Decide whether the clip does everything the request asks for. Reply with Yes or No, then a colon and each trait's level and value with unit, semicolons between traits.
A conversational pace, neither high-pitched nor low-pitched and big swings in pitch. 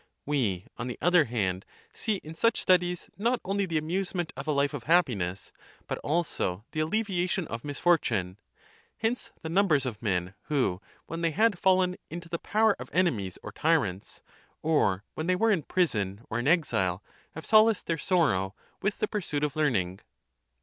Yes: average, 170 wpm; medium, 155 Hz; wide, 8.7 semitones